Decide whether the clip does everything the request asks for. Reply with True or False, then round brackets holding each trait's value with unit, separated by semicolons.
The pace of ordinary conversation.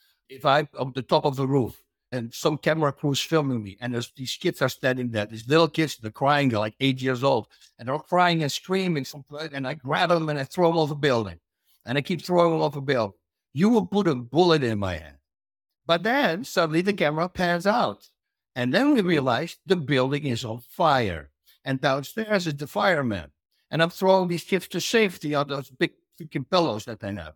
False (220 wpm)